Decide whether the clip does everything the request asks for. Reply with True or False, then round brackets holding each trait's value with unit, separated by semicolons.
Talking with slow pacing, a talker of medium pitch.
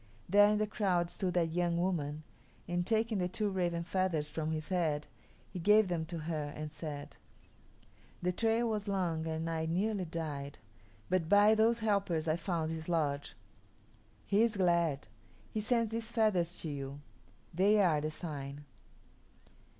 False (160 wpm; 175 Hz)